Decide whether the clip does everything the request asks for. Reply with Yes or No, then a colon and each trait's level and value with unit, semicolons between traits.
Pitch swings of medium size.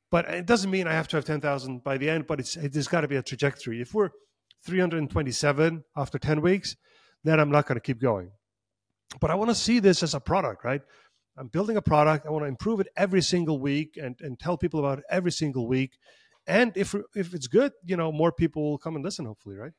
Yes: average, 4.2 semitones